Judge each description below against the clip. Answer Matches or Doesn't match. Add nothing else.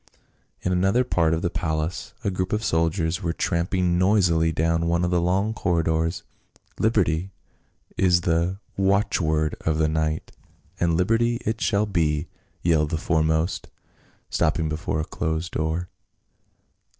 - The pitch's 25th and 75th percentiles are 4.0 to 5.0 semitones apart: Doesn't match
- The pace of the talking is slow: Doesn't match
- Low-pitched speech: Matches